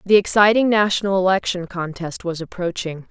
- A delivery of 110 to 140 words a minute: Yes, slow, 135 wpm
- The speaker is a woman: Yes, female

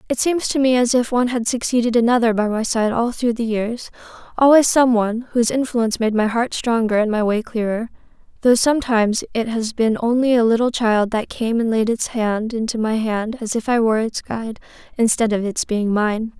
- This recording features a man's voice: No, female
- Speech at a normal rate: No, fast, 210 wpm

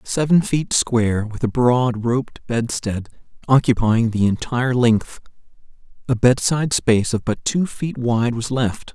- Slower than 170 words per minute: Yes, average, 150 wpm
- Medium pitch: No, low, 120 Hz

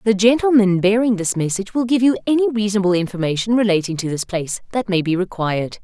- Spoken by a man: No, female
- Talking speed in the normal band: Yes, average, 195 wpm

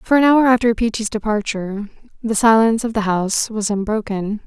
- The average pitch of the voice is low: No, high, 220 Hz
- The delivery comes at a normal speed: Yes, average, 175 wpm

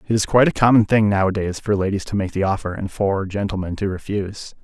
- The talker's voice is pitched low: Yes, low, 100 Hz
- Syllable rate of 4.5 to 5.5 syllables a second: No, 6.3 syllables/s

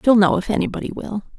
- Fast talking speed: Yes, fast, 215 wpm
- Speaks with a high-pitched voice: Yes, high, 210 Hz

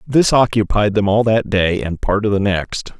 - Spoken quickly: Yes, fast, 220 wpm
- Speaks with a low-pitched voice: Yes, low, 105 Hz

